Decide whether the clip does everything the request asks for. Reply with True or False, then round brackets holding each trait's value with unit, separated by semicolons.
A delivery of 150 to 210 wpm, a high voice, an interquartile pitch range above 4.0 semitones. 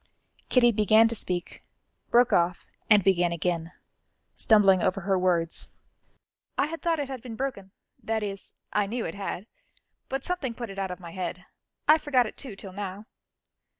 True (175 wpm; 205 Hz; 4.7 semitones)